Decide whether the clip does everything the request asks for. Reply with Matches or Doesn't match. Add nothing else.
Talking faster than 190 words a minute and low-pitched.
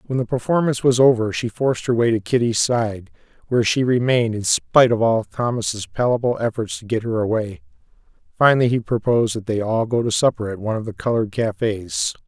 Matches